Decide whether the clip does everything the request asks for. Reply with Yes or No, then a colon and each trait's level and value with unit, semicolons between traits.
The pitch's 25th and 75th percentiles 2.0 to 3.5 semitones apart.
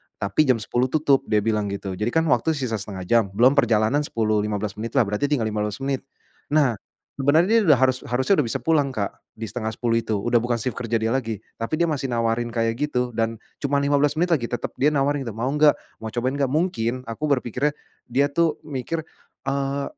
No: average, 4.1 semitones